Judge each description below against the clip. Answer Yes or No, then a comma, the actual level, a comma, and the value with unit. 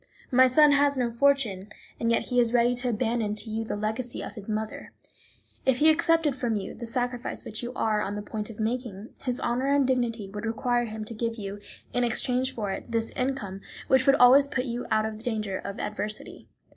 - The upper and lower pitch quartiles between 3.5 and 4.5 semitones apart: No, average, 2.9 semitones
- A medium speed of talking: No, fast, 215 wpm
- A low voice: No, high, 235 Hz